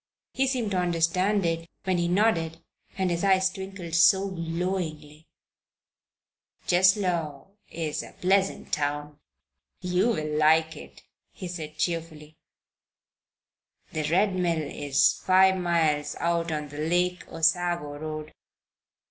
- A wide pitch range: No, average, 3.2 semitones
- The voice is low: No, medium, 170 Hz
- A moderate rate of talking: No, slow, 120 wpm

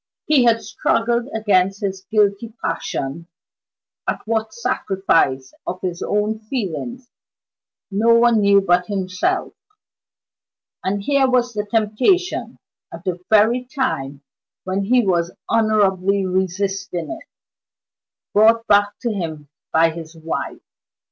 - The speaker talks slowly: Yes, slow, 115 wpm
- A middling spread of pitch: Yes, average, 3.8 semitones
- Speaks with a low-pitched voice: No, high, 205 Hz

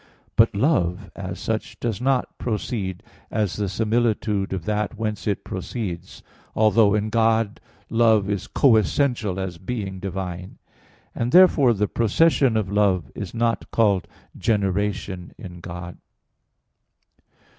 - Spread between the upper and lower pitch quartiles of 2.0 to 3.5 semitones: Yes, average, 3.2 semitones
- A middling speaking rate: No, slow, 125 wpm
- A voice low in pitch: Yes, low, 105 Hz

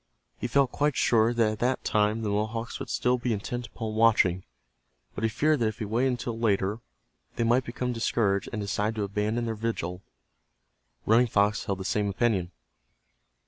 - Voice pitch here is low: Yes, low, 110 Hz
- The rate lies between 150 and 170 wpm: No, average, 185 wpm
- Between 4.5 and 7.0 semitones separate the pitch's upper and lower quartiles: No, narrow, 2.4 semitones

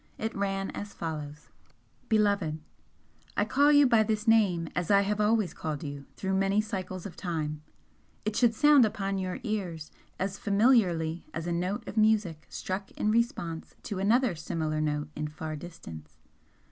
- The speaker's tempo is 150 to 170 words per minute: Yes, average, 160 wpm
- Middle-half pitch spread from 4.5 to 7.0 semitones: Yes, average, 4.9 semitones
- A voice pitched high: Yes, high, 195 Hz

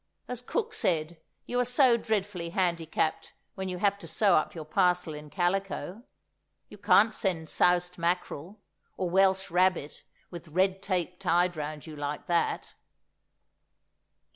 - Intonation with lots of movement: No, average, 2.8 semitones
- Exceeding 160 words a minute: No, average, 140 wpm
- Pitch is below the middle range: No, medium, 180 Hz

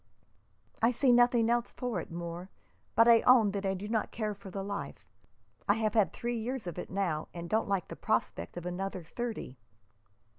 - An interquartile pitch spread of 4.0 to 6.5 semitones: Yes, average, 4.6 semitones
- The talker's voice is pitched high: Yes, high, 205 Hz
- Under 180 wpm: No, average, 195 wpm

